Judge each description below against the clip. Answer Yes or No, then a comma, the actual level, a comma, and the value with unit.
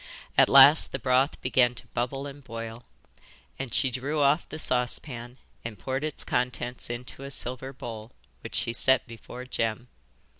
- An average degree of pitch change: No, narrow, 2.3 semitones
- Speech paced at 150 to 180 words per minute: Yes, average, 160 wpm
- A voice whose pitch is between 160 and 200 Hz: No, low, 125 Hz